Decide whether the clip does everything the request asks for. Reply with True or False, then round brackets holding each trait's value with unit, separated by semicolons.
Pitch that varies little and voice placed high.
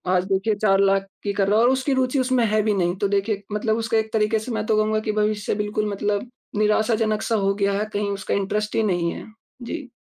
True (1.7 semitones; 210 Hz)